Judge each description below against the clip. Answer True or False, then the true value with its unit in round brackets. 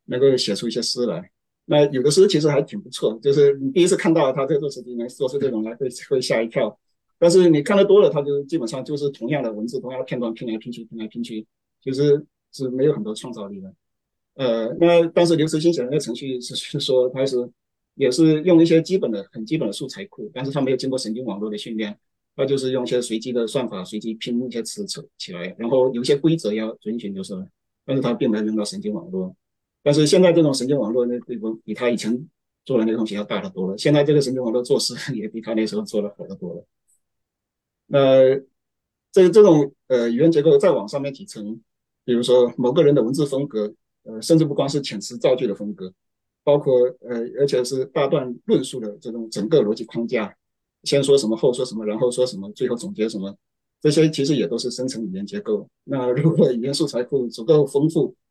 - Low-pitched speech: True (130 Hz)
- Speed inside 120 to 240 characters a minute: False (335 characters per minute)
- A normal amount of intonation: True (5.0 semitones)